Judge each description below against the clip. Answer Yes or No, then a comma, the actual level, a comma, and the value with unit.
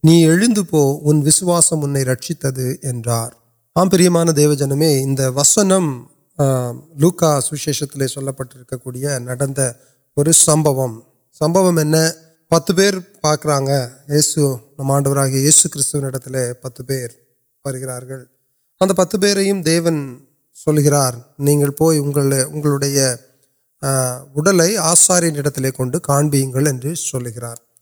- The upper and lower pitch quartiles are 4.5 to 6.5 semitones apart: No, average, 3.3 semitones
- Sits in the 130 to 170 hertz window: Yes, medium, 140 Hz